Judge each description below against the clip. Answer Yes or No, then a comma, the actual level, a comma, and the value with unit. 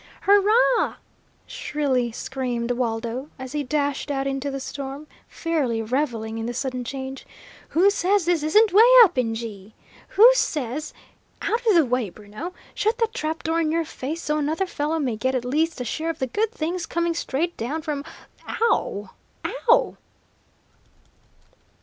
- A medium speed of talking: Yes, average, 160 wpm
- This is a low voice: No, very high, 290 Hz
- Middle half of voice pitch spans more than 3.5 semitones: Yes, average, 5.3 semitones